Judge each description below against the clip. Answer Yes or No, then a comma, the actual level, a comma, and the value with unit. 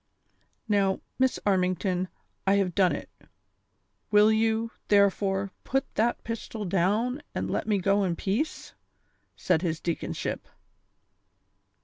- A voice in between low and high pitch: No, high, 200 Hz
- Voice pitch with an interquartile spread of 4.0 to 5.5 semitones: No, average, 2.9 semitones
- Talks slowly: Yes, slow, 125 wpm